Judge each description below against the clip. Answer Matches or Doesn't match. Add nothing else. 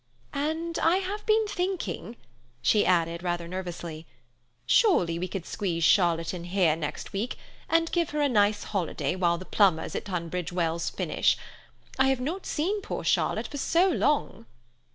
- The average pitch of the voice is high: Matches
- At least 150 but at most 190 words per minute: Matches